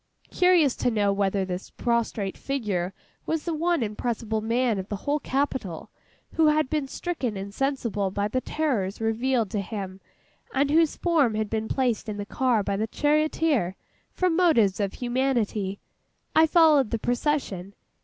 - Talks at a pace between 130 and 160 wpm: Yes, average, 155 wpm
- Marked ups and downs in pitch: Yes, wide, 6.3 semitones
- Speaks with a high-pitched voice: Yes, high, 235 Hz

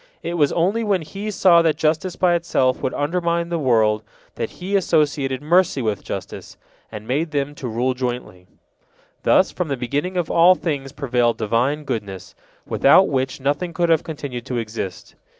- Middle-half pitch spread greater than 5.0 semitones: Yes, wide, 5.4 semitones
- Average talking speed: Yes, average, 170 wpm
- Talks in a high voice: No, medium, 145 Hz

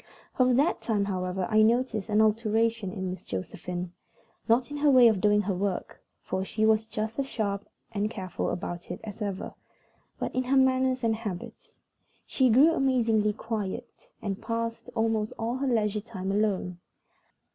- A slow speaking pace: No, average, 170 wpm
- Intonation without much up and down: No, average, 3.1 semitones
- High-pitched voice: Yes, high, 220 Hz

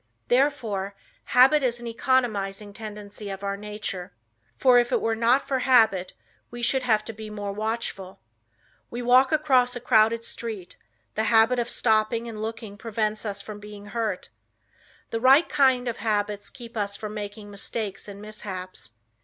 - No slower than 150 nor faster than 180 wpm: Yes, average, 160 wpm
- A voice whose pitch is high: Yes, high, 220 Hz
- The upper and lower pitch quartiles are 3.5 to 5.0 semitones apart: No, average, 2.8 semitones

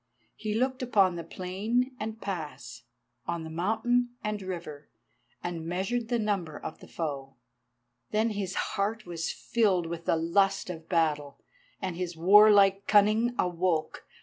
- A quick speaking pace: No, slow, 135 wpm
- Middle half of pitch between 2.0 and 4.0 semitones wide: No, average, 4.4 semitones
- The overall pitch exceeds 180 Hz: Yes, high, 190 Hz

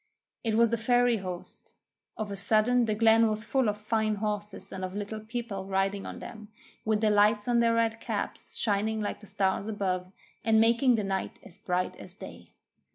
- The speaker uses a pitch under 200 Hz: No, high, 215 Hz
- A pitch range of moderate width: No, narrow, 2.2 semitones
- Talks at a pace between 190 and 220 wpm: Yes, average, 195 wpm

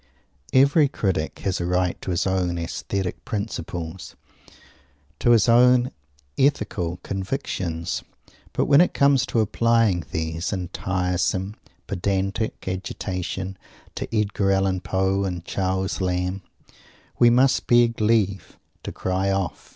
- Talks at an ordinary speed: No, slow, 120 wpm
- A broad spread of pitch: No, average, 3.7 semitones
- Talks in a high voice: No, very low, 95 Hz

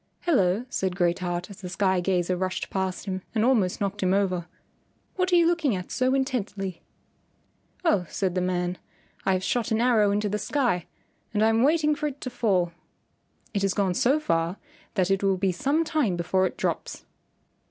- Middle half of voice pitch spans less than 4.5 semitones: No, average, 5.2 semitones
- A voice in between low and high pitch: No, high, 195 Hz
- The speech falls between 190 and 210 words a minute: Yes, average, 195 wpm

